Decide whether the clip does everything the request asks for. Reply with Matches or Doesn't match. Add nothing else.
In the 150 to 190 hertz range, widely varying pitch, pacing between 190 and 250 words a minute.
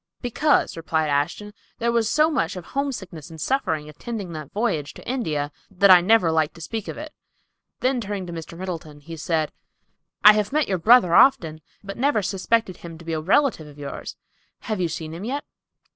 Matches